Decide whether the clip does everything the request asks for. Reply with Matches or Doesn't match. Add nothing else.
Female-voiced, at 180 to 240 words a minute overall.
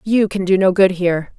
Doesn't match